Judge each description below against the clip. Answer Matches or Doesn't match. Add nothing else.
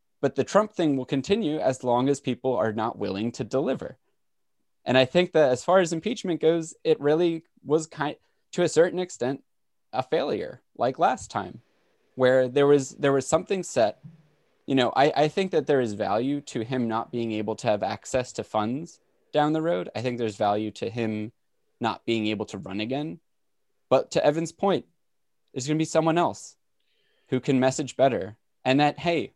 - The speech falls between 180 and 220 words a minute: Matches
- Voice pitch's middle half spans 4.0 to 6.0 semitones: Matches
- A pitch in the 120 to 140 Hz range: Matches